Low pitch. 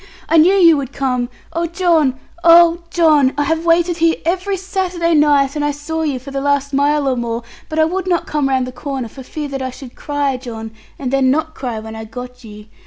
No: very high, 285 Hz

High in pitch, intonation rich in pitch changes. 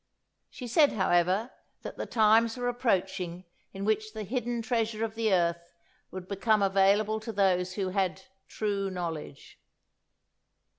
No: high, 205 Hz; average, 3.3 semitones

